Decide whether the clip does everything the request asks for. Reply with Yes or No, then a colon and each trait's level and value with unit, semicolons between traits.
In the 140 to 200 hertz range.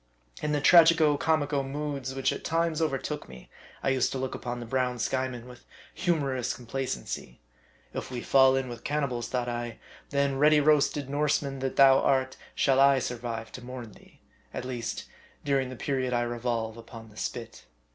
No: low, 130 Hz